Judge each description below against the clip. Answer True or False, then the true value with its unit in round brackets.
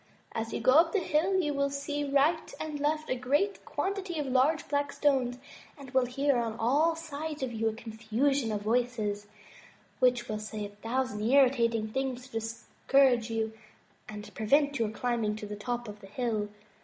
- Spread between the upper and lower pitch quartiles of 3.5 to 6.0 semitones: True (4.4 semitones)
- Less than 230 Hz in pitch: False (250 Hz)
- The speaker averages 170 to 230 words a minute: True (180 wpm)